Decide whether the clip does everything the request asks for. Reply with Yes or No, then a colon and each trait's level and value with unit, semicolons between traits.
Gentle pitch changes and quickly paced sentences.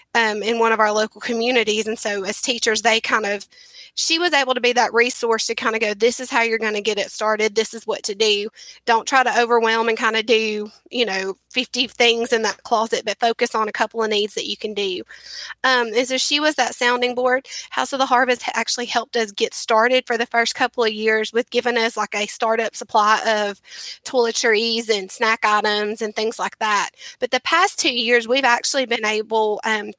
Yes: narrow, 2.1 semitones; fast, 230 wpm